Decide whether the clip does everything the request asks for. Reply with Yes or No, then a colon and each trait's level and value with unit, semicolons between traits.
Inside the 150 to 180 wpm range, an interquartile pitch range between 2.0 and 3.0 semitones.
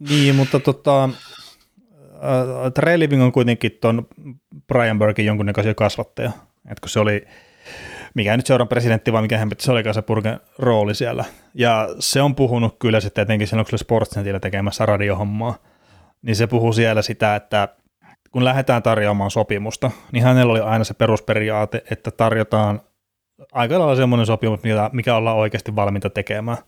Yes: fast, 155 wpm; narrow, 2.6 semitones